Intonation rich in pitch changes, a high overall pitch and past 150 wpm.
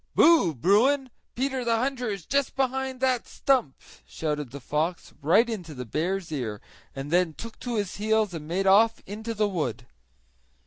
Yes: wide, 7.7 semitones; high, 205 Hz; average, 170 wpm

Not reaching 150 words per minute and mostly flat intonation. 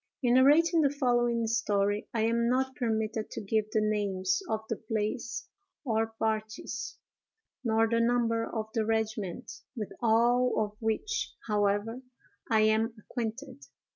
Yes: average, 140 wpm; narrow, 2.0 semitones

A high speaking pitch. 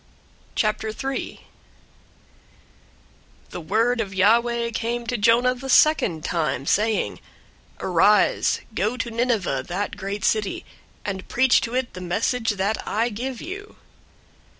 Yes: high, 225 Hz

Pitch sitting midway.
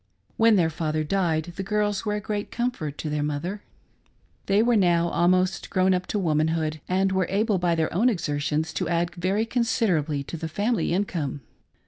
Yes: medium, 180 Hz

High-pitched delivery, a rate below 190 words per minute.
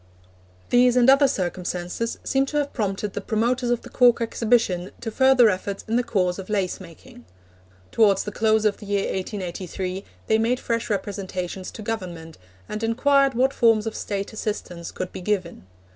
Yes: high, 215 Hz; average, 175 wpm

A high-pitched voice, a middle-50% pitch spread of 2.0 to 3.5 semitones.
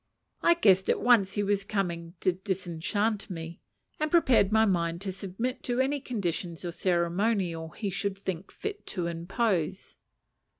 No: high, 195 Hz; average, 4.3 semitones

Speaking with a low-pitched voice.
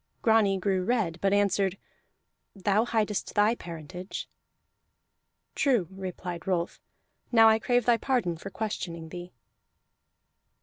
No: high, 195 Hz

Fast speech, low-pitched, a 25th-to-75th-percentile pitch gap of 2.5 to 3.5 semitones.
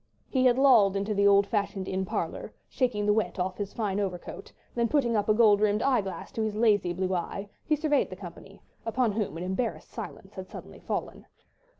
No: fast, 210 wpm; high, 210 Hz; average, 3.2 semitones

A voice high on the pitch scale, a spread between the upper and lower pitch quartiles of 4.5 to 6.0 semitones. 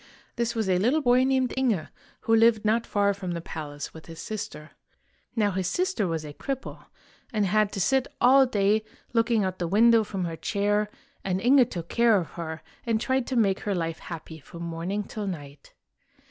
Yes: high, 205 Hz; average, 5.3 semitones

